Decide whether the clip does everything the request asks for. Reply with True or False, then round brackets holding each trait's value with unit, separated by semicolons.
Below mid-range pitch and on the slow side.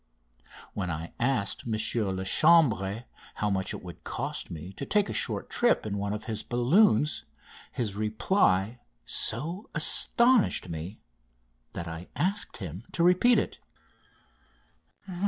True (110 Hz; 130 wpm)